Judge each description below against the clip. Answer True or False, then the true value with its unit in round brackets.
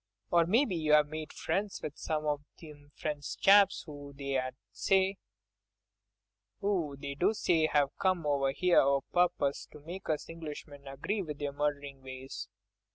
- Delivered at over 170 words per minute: False (140 wpm)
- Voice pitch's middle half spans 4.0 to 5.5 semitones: False (3.4 semitones)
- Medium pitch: True (150 Hz)